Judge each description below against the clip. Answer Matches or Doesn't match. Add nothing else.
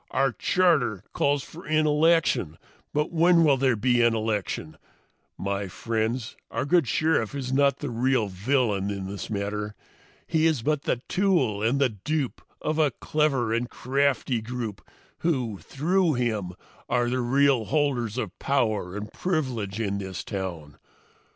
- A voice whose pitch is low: Matches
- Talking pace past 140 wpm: Matches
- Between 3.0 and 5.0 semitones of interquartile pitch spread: Doesn't match